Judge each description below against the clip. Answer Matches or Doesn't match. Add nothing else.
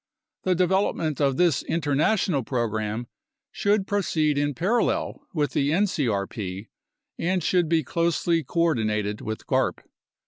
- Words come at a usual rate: Doesn't match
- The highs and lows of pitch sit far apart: Matches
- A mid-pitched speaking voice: Matches